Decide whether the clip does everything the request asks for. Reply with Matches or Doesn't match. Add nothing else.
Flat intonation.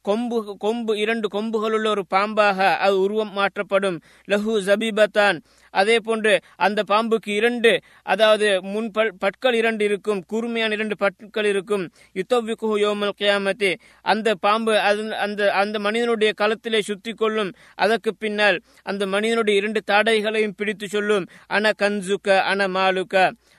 Matches